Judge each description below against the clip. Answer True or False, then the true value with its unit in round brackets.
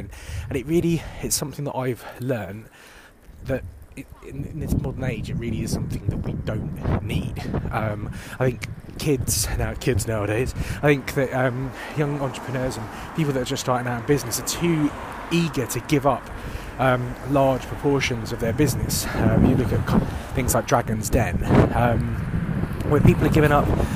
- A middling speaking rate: True (175 wpm)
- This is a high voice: False (125 Hz)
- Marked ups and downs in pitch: False (4.0 semitones)